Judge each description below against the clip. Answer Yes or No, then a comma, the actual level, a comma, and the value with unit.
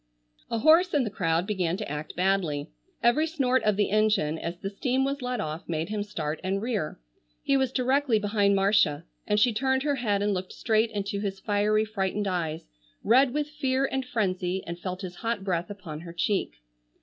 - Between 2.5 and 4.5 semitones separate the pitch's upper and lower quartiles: No, wide, 5.4 semitones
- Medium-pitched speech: No, high, 205 Hz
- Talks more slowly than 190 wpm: No, average, 195 wpm